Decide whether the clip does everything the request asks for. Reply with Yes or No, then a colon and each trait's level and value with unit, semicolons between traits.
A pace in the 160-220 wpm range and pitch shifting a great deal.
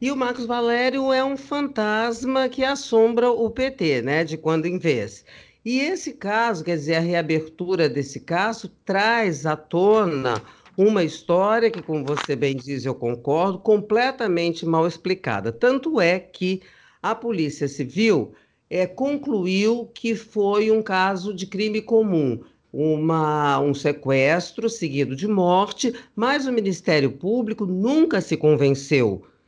No: average, 140 wpm; wide, 6.6 semitones